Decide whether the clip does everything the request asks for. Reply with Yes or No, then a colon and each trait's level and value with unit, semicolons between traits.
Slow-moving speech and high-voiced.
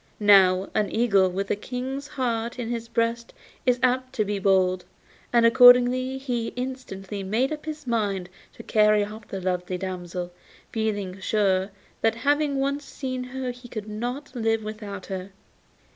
No: average, 160 wpm; high, 225 Hz